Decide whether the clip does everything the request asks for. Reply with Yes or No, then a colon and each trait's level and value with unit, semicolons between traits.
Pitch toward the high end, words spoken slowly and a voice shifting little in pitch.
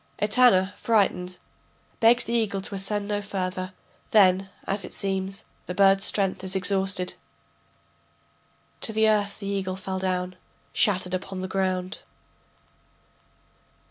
Yes: high, 195 Hz; slow, 125 wpm; narrow, 1.6 semitones